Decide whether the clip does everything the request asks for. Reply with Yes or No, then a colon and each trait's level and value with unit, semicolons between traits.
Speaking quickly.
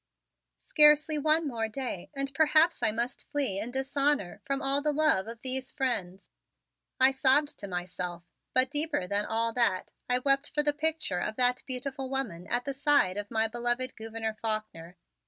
No: average, 175 wpm